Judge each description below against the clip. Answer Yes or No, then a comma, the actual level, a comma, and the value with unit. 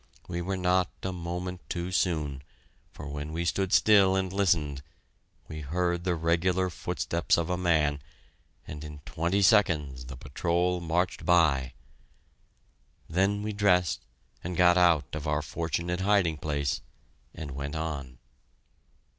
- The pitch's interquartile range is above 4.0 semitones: No, average, 3.3 semitones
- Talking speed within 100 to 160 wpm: Yes, average, 140 wpm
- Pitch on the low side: Yes, very low, 85 Hz